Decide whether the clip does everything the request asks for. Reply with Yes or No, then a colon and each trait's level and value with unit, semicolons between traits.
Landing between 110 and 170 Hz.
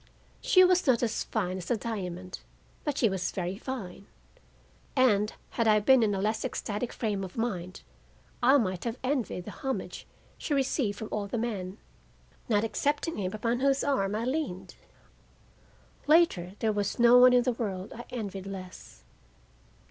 No: high, 220 Hz